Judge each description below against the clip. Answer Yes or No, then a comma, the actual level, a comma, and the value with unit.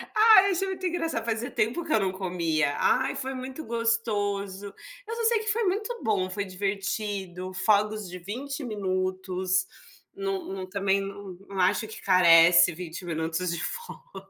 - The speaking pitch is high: Yes, high, 200 Hz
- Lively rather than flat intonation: Yes, wide, 6.3 semitones